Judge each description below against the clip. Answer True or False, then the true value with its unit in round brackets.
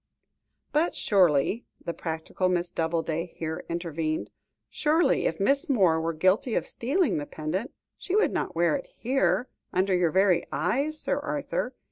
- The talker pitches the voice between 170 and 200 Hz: True (185 Hz)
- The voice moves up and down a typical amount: False (8.2 semitones)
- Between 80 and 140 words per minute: False (150 wpm)